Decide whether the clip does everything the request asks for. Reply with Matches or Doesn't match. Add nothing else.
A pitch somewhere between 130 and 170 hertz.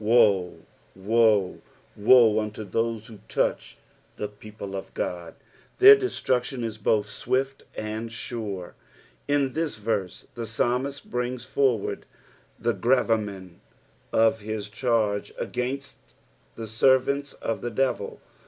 Doesn't match